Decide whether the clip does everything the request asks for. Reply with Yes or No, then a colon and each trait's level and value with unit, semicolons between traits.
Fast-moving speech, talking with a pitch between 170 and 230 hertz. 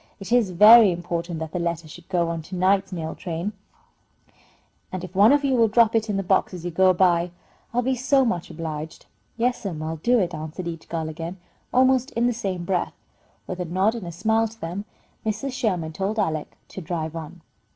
Yes: fast, 210 wpm; medium, 185 Hz